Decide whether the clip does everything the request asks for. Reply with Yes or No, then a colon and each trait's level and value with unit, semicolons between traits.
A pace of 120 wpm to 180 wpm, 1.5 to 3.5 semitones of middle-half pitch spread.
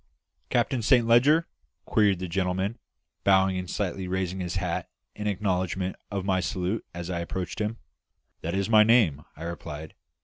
Yes: average, 160 wpm; average, 2.9 semitones